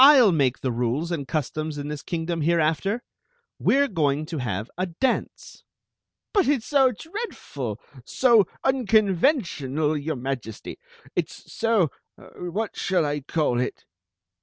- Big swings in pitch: Yes, wide, 7.9 semitones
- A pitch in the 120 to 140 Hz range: No, medium, 165 Hz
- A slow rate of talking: No, average, 150 wpm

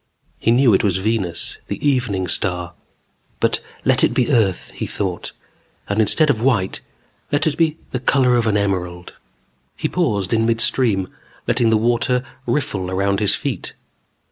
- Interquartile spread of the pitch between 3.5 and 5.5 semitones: Yes, average, 4.6 semitones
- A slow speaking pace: No, average, 165 wpm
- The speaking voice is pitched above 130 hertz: No, low, 110 Hz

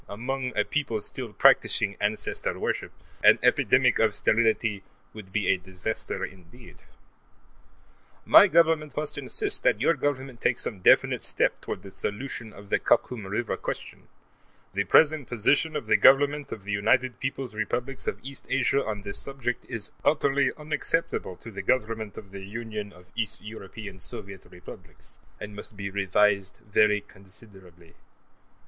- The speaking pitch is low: Yes, low, 110 Hz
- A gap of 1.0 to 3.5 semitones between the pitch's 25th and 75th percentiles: No, average, 5.1 semitones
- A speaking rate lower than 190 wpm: Yes, average, 150 wpm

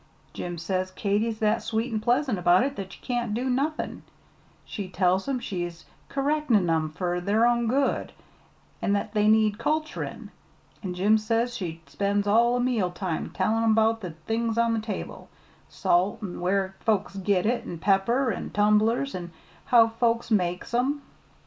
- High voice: Yes, high, 215 Hz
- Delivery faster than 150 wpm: Yes, average, 170 wpm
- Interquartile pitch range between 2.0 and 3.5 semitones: No, average, 4.0 semitones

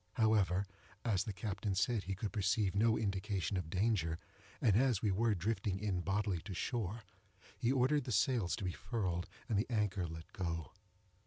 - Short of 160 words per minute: No, average, 175 wpm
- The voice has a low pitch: Yes, low, 100 Hz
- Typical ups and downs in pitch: Yes, average, 3.3 semitones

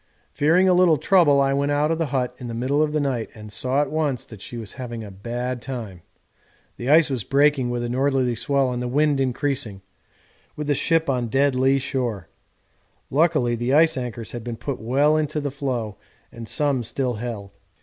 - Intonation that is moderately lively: Yes, average, 3.4 semitones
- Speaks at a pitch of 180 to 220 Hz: No, low, 130 Hz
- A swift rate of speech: Yes, fast, 210 wpm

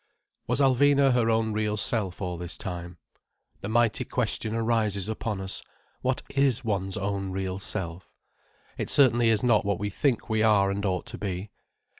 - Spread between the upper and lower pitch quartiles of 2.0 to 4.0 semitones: Yes, average, 3.2 semitones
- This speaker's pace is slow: No, average, 170 wpm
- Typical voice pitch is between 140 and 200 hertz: No, low, 105 Hz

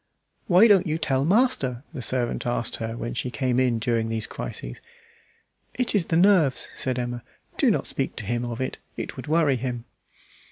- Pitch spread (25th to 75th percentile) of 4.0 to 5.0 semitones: No, wide, 5.4 semitones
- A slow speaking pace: No, average, 190 wpm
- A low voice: Yes, low, 130 Hz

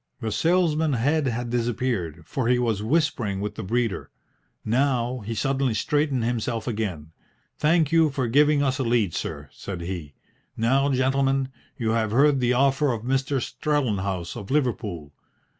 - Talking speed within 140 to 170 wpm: Yes, average, 155 wpm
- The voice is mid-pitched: No, low, 125 Hz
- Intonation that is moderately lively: Yes, average, 4.1 semitones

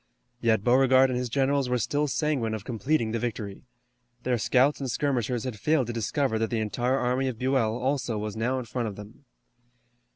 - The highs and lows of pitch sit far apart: No, average, 3.0 semitones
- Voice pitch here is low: Yes, low, 125 Hz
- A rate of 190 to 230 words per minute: Yes, average, 195 wpm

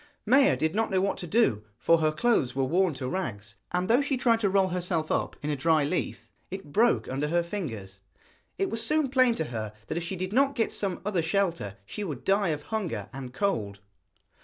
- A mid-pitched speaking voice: Yes, medium, 175 Hz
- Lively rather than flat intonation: Yes, wide, 6.9 semitones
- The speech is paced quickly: Yes, fast, 220 wpm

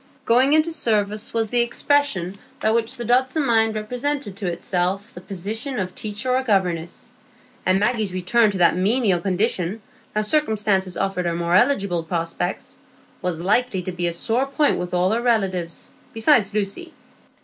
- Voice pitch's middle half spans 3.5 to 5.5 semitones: Yes, average, 4.7 semitones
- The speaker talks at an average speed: Yes, average, 160 wpm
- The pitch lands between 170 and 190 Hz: No, high, 210 Hz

